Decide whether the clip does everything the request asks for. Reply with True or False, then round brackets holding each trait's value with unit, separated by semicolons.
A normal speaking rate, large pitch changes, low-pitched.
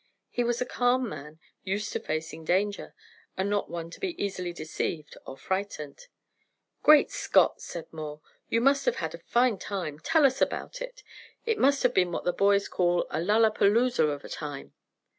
False (180 wpm; 7.2 semitones; 200 Hz)